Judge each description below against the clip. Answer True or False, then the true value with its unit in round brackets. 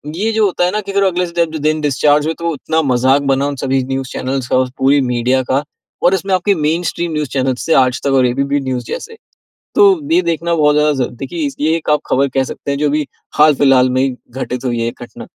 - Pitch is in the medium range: True (145 Hz)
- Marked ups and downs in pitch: False (4.2 semitones)